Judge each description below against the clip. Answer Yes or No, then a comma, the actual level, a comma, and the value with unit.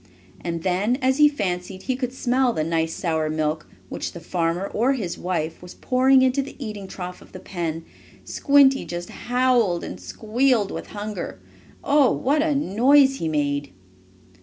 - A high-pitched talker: Yes, high, 205 Hz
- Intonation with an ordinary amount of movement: No, wide, 7.4 semitones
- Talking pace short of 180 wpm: Yes, average, 165 wpm